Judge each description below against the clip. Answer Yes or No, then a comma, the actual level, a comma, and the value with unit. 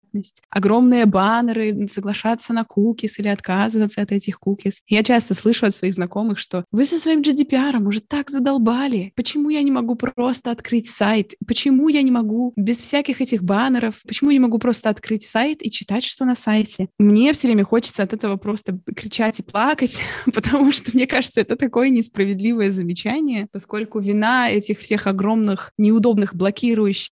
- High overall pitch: Yes, high, 220 Hz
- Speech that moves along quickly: Yes, fast, 170 wpm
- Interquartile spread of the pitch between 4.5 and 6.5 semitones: No, average, 3.2 semitones